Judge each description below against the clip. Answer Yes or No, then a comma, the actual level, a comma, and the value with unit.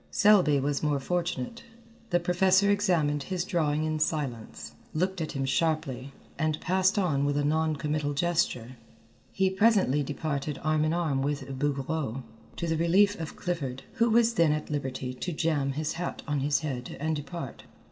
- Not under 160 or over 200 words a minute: Yes, average, 165 wpm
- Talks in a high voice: No, medium, 155 Hz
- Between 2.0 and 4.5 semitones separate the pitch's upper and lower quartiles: Yes, average, 3.7 semitones